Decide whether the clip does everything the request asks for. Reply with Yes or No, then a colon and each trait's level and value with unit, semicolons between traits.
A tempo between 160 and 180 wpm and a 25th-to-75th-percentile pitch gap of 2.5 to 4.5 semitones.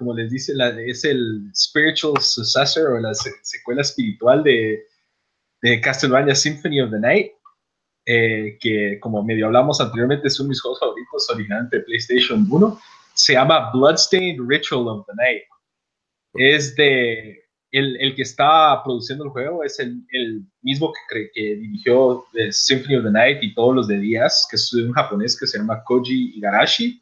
Yes: average, 170 wpm; average, 4.0 semitones